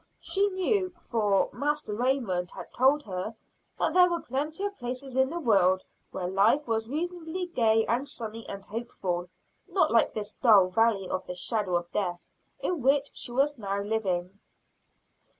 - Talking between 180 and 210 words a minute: No, average, 165 wpm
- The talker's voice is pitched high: Yes, high, 230 Hz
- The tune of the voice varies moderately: No, wide, 6.8 semitones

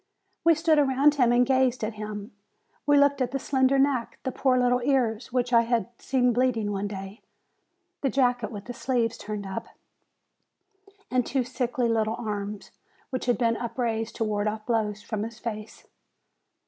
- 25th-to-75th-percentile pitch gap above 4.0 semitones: No, average, 3.1 semitones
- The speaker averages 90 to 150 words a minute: No, average, 175 wpm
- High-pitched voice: Yes, high, 240 Hz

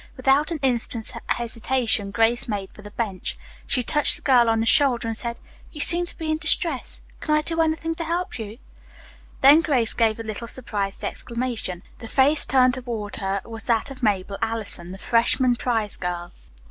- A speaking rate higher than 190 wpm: No, average, 185 wpm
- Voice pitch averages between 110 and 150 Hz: No, high, 235 Hz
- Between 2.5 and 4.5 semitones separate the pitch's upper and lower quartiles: Yes, average, 3.9 semitones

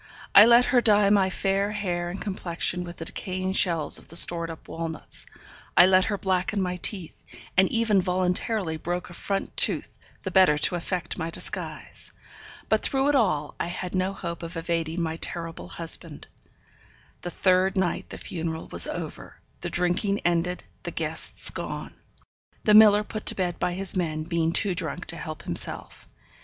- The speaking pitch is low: No, medium, 180 Hz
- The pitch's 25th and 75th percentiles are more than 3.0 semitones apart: No, average, 2.7 semitones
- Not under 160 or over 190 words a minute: Yes, average, 175 wpm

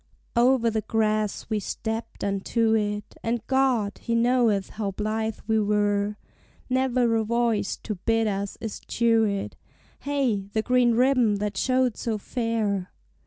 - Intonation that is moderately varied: No, narrow, 2.3 semitones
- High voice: Yes, high, 225 Hz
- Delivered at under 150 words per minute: Yes, average, 140 wpm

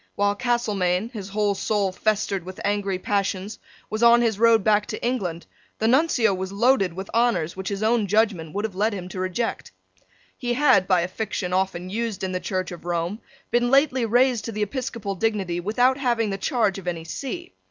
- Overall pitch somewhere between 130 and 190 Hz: No, high, 205 Hz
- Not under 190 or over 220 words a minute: Yes, average, 195 wpm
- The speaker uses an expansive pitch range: No, average, 3.8 semitones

